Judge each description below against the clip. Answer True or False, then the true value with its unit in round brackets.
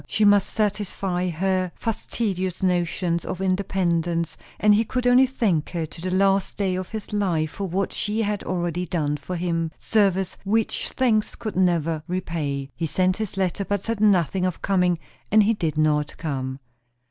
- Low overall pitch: False (185 Hz)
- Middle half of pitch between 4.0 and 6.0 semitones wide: False (3.3 semitones)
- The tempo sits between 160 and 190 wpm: True (170 wpm)